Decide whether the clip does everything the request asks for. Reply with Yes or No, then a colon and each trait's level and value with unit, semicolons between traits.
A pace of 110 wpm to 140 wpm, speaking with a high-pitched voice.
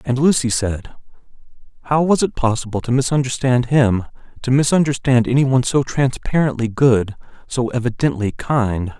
No: slow, 135 wpm; low, 125 Hz